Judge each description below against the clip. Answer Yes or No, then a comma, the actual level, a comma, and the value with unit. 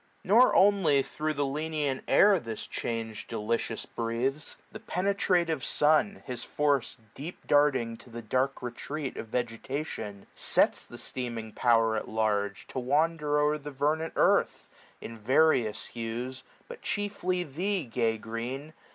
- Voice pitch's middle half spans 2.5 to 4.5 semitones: No, average, 5.3 semitones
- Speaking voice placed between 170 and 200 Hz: No, low, 135 Hz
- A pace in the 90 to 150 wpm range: Yes, average, 140 wpm